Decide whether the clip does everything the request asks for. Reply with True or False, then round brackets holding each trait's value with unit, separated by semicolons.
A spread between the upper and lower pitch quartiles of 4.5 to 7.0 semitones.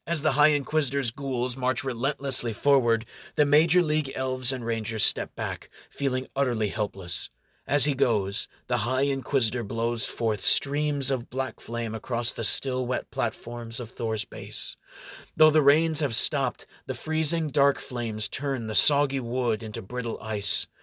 False (3.5 semitones)